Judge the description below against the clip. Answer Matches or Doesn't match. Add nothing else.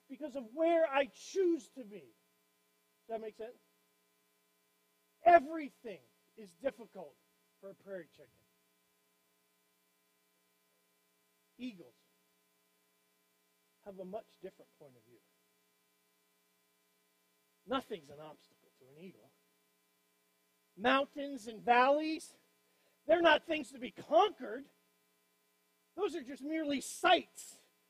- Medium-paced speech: Doesn't match